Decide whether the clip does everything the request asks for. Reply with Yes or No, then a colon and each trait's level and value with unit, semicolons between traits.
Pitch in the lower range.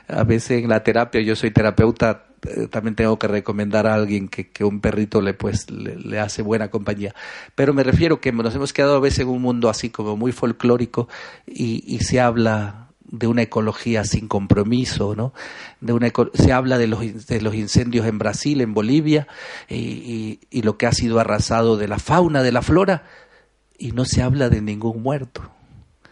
Yes: low, 115 Hz